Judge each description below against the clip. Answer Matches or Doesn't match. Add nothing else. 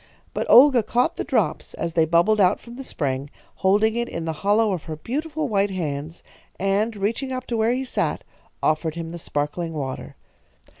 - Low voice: Doesn't match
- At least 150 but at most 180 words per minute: Doesn't match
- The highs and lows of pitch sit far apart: Matches